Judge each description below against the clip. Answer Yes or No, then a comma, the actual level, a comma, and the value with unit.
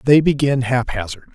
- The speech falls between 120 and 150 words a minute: Yes, slow, 135 wpm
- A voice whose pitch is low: Yes, low, 125 Hz